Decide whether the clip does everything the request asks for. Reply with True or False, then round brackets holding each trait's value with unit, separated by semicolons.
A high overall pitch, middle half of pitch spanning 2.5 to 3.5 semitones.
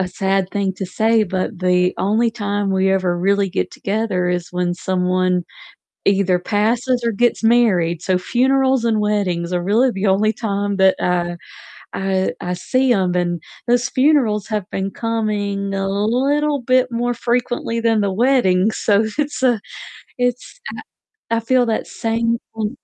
False (205 Hz; 3.9 semitones)